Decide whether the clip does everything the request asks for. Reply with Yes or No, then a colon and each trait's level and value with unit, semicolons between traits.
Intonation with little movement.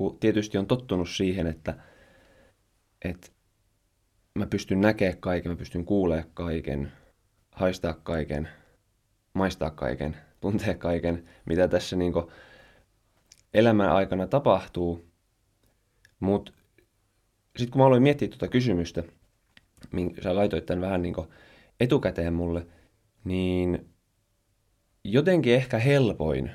No: average, 4.0 semitones